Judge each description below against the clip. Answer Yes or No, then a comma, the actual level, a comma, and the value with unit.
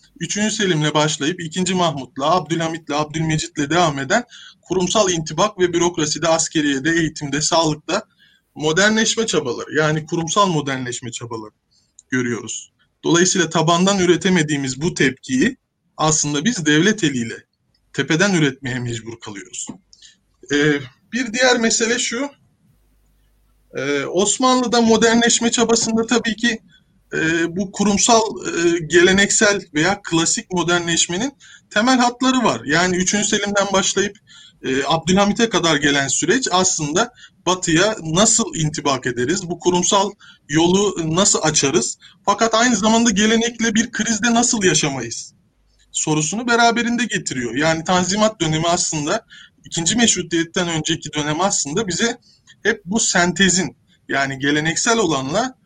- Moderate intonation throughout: No, wide, 5.7 semitones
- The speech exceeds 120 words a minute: No, average, 110 wpm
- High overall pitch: No, medium, 175 Hz